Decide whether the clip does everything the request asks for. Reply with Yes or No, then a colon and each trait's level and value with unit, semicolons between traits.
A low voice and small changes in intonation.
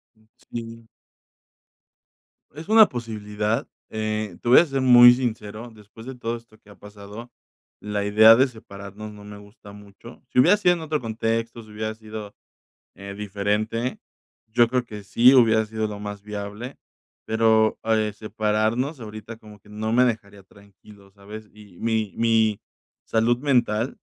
Yes: low, 110 Hz; narrow, 2.2 semitones